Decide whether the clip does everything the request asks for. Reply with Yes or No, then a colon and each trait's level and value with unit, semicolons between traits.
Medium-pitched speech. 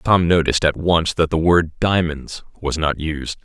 No: very low, 80 Hz